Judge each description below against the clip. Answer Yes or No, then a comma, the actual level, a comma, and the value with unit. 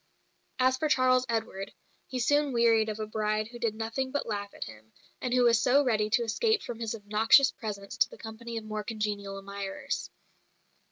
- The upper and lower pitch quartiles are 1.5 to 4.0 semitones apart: Yes, average, 3.0 semitones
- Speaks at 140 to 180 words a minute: No, average, 190 wpm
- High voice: Yes, high, 225 Hz